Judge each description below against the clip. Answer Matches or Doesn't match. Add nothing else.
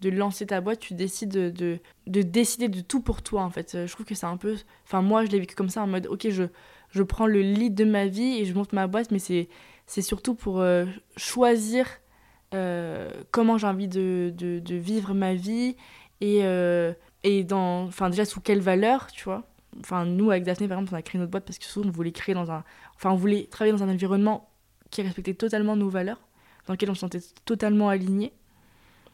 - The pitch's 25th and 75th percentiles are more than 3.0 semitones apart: Doesn't match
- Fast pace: Matches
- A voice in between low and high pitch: Doesn't match